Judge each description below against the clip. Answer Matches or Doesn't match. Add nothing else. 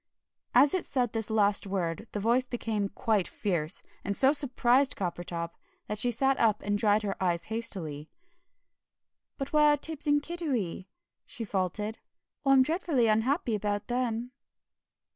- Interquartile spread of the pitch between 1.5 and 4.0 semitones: Doesn't match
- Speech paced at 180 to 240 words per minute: Doesn't match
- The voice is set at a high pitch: Matches